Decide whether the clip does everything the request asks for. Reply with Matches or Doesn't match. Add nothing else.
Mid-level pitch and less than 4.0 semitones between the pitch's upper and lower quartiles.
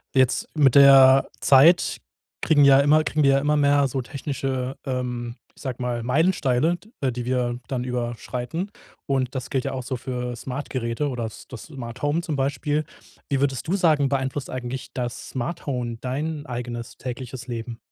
Doesn't match